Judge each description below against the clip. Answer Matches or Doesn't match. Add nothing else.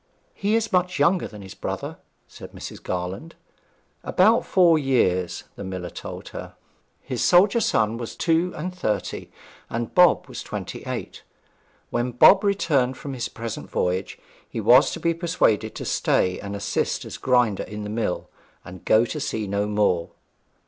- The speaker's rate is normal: Matches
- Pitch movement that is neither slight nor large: Doesn't match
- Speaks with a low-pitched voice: Matches